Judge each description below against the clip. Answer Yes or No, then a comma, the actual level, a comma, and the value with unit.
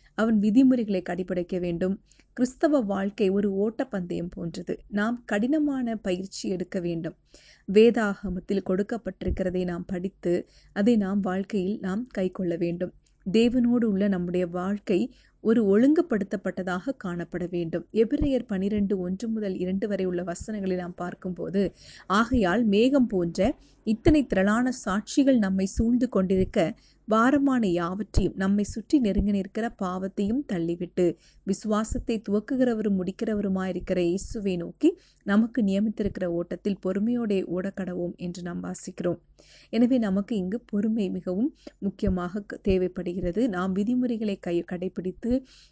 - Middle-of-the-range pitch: No, high, 200 Hz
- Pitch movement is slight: No, average, 3.7 semitones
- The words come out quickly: No, average, 110 wpm